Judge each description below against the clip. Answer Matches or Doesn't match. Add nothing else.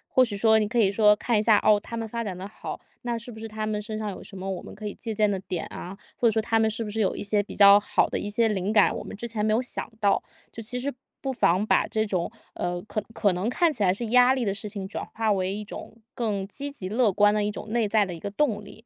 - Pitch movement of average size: Doesn't match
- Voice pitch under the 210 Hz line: Doesn't match